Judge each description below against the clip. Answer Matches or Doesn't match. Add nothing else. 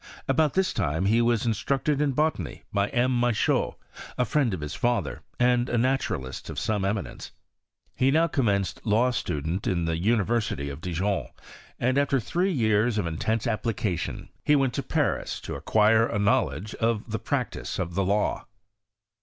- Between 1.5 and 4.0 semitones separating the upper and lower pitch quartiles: Doesn't match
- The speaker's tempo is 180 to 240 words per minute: Doesn't match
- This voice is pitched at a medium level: Doesn't match